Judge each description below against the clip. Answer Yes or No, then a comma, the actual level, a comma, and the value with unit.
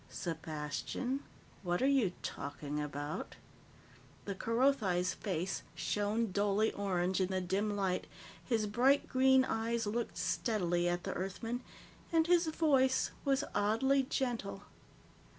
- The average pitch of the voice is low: No, high, 205 Hz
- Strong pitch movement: Yes, wide, 6.2 semitones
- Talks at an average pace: No, slow, 120 wpm